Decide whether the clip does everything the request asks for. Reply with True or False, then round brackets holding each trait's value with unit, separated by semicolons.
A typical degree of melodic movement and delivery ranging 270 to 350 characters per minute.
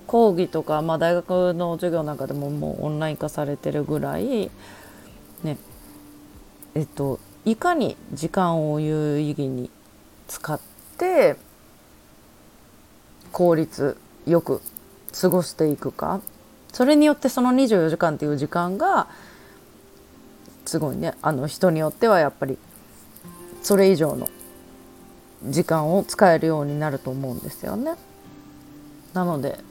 False (3.8 semitones; 240 characters per minute)